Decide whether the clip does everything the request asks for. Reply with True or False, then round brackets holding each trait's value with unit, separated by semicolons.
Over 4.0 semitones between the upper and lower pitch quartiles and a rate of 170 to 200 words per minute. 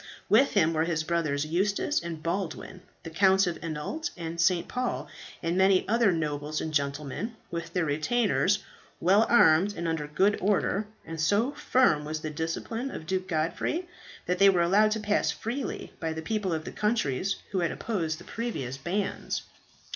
True (4.5 semitones; 175 wpm)